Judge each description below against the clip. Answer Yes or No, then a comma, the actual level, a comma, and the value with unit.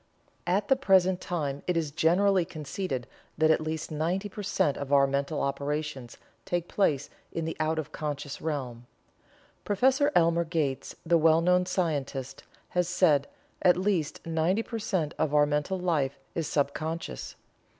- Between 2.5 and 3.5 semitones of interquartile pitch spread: No, average, 3.9 semitones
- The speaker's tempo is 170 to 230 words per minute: No, average, 160 wpm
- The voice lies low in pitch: No, medium, 160 Hz